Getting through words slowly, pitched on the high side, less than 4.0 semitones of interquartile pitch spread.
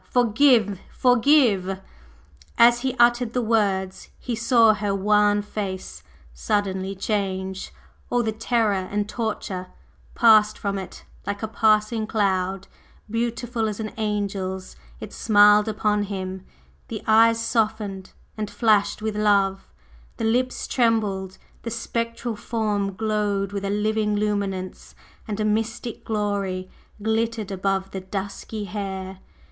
Yes: slow, 125 wpm; high, 210 Hz; narrow, 2.4 semitones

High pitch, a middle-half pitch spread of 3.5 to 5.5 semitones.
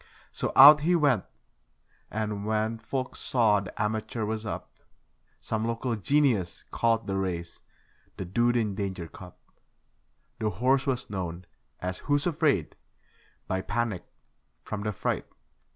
No: low, 110 Hz; average, 4.1 semitones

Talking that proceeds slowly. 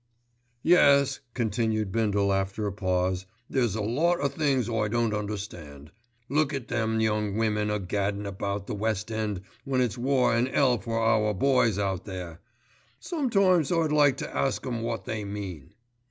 No: average, 165 wpm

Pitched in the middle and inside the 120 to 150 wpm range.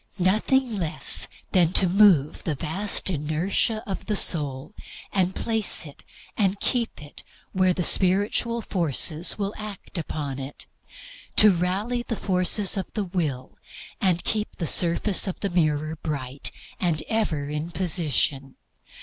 Yes: medium, 180 Hz; average, 145 wpm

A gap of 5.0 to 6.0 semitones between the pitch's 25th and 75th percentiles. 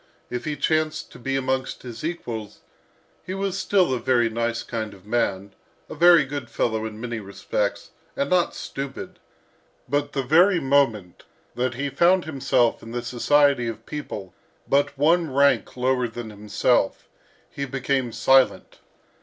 No: average, 3.7 semitones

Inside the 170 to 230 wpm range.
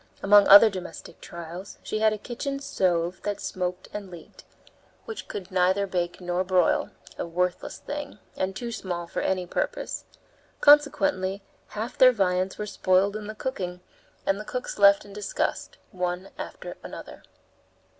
No: average, 155 wpm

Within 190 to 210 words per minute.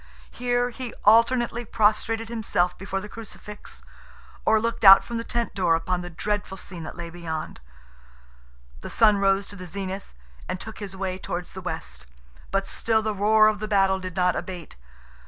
No: average, 175 wpm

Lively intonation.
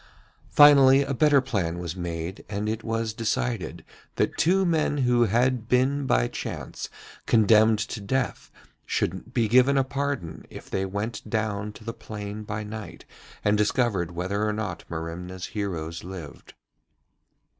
No: average, 4.7 semitones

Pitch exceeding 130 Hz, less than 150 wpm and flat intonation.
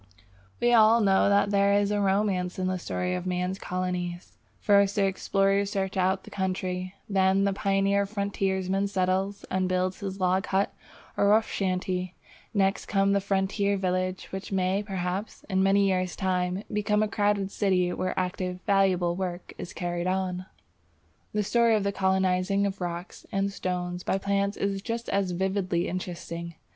No: high, 190 Hz; average, 165 wpm; narrow, 1.5 semitones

